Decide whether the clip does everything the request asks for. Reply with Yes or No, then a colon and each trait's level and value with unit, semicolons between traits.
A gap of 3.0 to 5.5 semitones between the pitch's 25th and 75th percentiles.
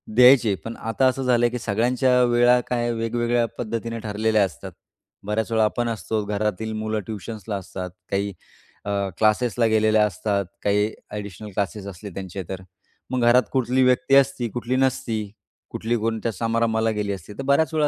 No: narrow, 2.6 semitones